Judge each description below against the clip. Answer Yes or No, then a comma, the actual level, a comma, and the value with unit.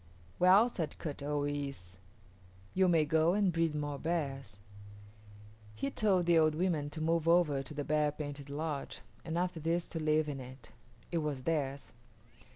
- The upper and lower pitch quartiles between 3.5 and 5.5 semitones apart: No, average, 2.8 semitones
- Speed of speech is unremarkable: Yes, average, 165 wpm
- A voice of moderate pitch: Yes, medium, 155 Hz